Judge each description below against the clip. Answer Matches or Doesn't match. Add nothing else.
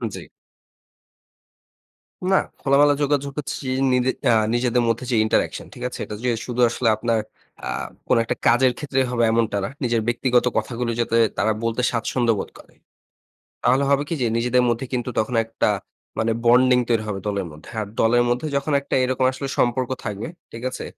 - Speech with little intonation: Matches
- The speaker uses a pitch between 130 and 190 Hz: Doesn't match